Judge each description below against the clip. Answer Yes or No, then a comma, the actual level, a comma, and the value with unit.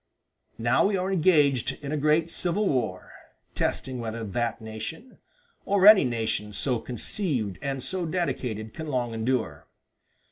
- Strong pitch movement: Yes, wide, 6.7 semitones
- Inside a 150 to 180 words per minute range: No, average, 140 wpm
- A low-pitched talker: Yes, low, 130 Hz